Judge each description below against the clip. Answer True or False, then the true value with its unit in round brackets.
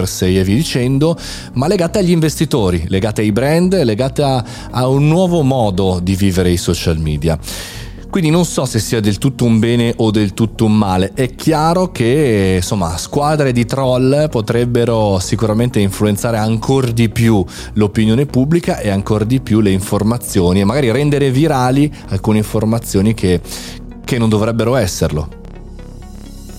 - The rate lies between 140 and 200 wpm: True (155 wpm)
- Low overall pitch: True (110 Hz)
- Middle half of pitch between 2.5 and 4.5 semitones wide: False (5.4 semitones)